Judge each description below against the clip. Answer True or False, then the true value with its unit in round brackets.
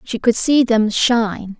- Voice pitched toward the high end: True (225 Hz)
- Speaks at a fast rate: False (190 wpm)